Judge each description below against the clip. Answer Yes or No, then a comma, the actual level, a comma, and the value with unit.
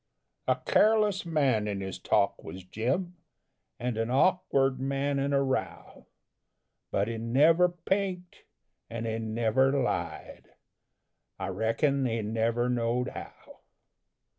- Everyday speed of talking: No, slow, 120 wpm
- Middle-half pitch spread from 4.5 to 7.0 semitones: Yes, average, 5.1 semitones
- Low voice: Yes, low, 130 Hz